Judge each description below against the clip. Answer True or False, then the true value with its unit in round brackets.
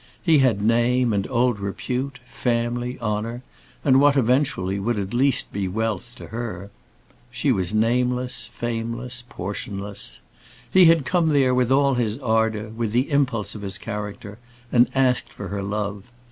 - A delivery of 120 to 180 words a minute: True (155 wpm)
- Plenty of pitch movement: False (3.4 semitones)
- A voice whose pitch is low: True (120 Hz)